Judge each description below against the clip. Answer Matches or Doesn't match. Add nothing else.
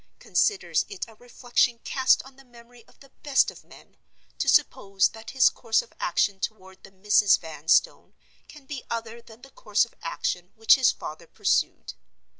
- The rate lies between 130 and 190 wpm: Matches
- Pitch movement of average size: Matches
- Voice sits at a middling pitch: Doesn't match